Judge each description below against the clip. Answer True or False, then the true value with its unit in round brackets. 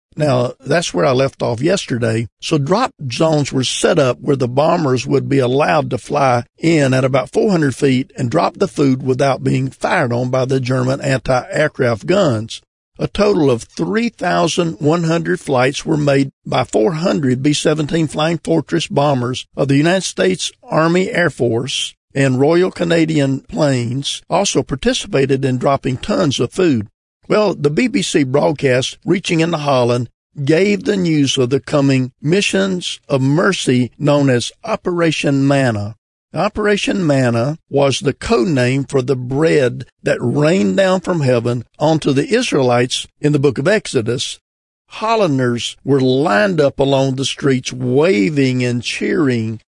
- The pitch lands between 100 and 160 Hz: True (140 Hz)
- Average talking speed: True (145 wpm)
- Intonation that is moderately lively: True (4.3 semitones)